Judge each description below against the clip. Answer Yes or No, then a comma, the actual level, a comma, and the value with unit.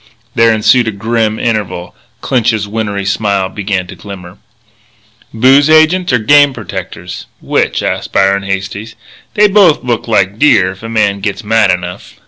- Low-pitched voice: Yes, low, 105 Hz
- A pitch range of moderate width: Yes, average, 3.4 semitones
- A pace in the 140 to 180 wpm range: Yes, average, 150 wpm